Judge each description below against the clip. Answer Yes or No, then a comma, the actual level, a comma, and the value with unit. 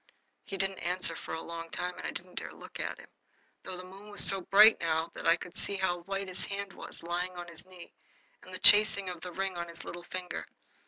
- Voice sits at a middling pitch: Yes, medium, 180 Hz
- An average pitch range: No, narrow, 2.0 semitones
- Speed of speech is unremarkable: No, fast, 245 wpm